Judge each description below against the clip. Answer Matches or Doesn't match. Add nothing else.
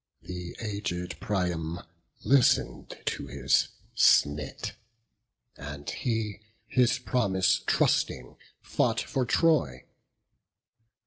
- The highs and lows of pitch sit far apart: Matches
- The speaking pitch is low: Matches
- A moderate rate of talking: Doesn't match